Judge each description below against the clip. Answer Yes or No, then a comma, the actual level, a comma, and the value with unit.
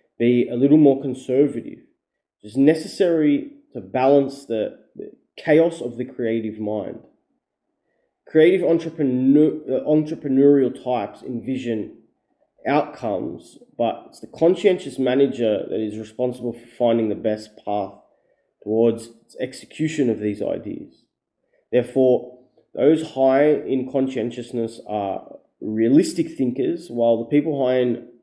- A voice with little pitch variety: No, average, 3.6 semitones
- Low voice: Yes, low, 125 Hz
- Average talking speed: No, slow, 115 wpm